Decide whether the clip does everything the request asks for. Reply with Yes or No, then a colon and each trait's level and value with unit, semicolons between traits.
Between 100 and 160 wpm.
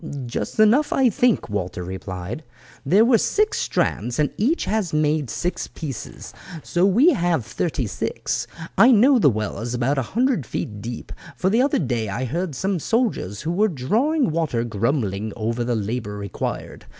No: average, 175 wpm